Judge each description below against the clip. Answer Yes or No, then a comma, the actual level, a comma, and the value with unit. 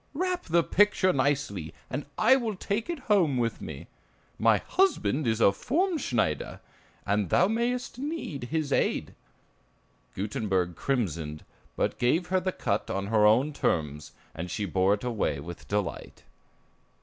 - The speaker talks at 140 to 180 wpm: Yes, average, 145 wpm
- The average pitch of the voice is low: Yes, low, 130 Hz